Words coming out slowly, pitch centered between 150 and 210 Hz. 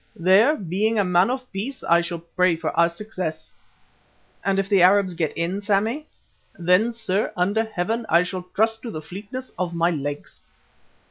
No: average, 175 wpm; high, 190 Hz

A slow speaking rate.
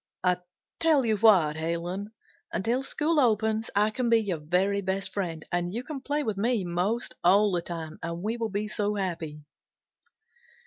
No: average, 175 wpm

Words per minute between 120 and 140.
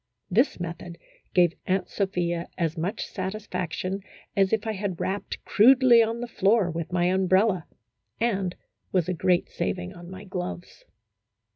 No: average, 150 wpm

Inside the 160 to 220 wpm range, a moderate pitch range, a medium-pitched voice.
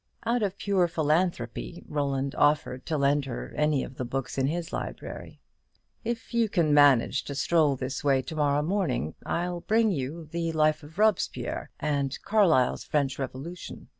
Yes: average, 165 wpm; average, 4.2 semitones; medium, 150 Hz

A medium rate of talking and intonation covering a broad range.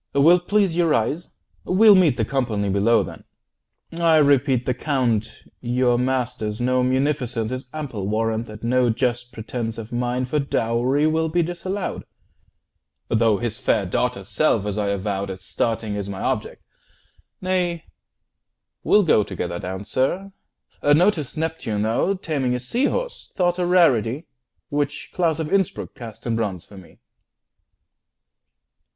Yes: average, 145 wpm; wide, 6.2 semitones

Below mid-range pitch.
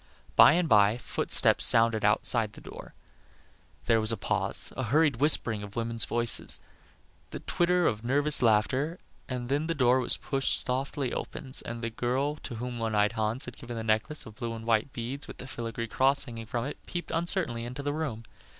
Yes: low, 120 Hz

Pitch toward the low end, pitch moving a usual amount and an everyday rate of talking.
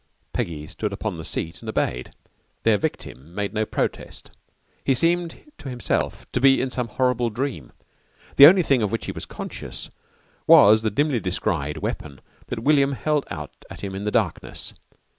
No: low, 115 Hz; wide, 6.3 semitones; average, 175 wpm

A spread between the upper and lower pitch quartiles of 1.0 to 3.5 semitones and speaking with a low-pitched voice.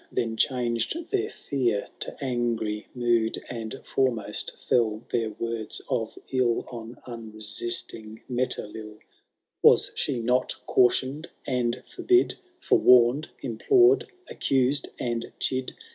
Yes: narrow, 2.4 semitones; low, 120 Hz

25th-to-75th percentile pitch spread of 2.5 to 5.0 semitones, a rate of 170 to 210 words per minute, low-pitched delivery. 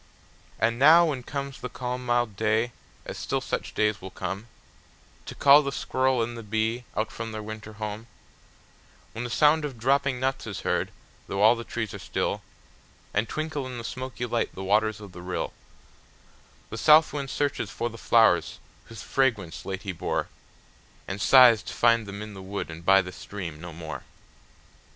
Yes: average, 4.1 semitones; average, 175 wpm; low, 115 Hz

